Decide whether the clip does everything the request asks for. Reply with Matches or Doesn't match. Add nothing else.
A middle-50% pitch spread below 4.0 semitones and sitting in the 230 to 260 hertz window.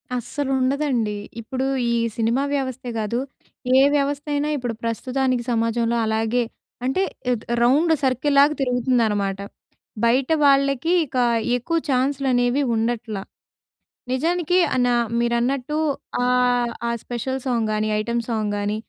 Matches